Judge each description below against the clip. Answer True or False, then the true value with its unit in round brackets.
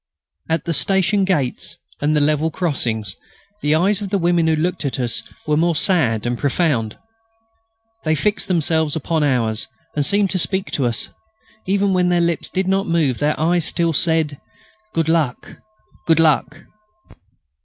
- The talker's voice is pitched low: False (160 Hz)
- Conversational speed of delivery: True (165 wpm)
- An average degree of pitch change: True (3.7 semitones)